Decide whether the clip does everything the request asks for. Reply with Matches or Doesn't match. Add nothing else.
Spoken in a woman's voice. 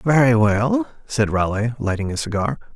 Doesn't match